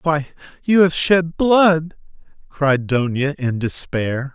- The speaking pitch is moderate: Yes, medium, 150 Hz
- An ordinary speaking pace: No, slow, 125 wpm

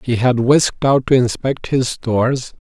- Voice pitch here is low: Yes, low, 125 Hz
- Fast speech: No, average, 180 wpm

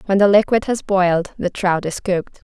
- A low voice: No, high, 190 Hz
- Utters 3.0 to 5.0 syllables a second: No, 5.3 syllables/s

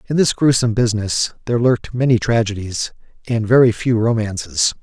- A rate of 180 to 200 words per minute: No, average, 150 wpm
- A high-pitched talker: No, low, 115 Hz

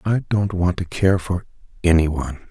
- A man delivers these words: Yes, male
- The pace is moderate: Yes, average, 170 wpm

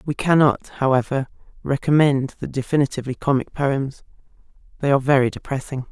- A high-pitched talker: No, low, 135 Hz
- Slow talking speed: Yes, slow, 120 wpm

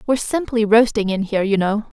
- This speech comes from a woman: Yes, female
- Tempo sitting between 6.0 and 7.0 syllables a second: Yes, 6.4 syllables/s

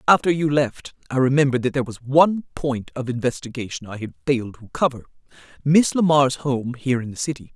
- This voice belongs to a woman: Yes, female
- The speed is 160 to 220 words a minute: Yes, average, 185 wpm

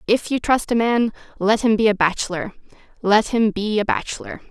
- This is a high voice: Yes, high, 215 Hz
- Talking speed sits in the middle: Yes, average, 185 wpm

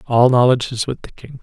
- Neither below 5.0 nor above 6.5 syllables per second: Yes, 6.2 syllables/s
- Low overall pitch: Yes, low, 125 Hz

